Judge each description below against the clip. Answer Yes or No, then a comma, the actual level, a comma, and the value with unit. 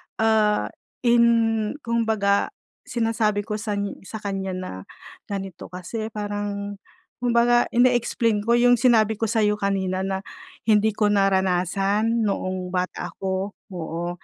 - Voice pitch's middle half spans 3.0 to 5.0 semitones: No, narrow, 2.6 semitones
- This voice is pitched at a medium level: No, high, 210 Hz